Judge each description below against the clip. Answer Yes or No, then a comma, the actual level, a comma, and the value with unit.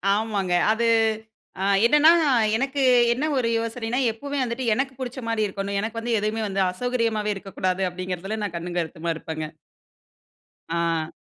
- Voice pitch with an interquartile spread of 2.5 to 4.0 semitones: No, average, 4.5 semitones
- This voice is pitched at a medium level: No, high, 215 Hz